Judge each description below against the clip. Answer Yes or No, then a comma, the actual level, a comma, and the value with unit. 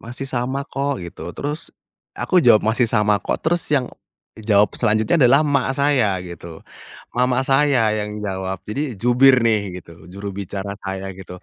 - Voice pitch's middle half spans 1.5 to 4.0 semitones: No, average, 5.3 semitones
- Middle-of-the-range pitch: No, low, 110 Hz